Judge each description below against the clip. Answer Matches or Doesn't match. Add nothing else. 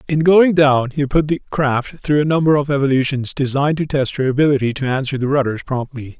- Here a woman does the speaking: Doesn't match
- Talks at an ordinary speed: Doesn't match